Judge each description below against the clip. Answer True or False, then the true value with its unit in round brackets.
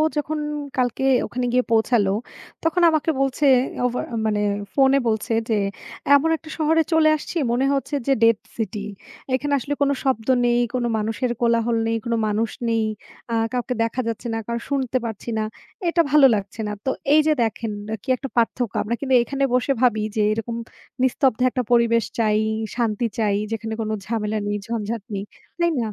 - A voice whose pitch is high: True (235 Hz)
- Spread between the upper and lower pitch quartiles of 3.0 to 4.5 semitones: True (3.4 semitones)